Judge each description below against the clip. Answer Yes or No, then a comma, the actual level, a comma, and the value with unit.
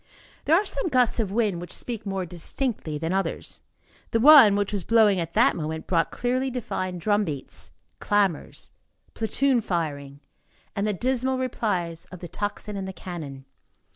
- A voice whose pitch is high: Yes, high, 200 Hz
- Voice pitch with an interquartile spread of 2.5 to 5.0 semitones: No, wide, 5.6 semitones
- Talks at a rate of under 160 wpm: No, average, 165 wpm